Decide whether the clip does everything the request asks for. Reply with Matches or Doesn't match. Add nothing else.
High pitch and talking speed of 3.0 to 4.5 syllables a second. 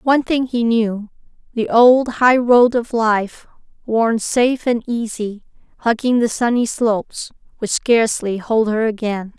Matches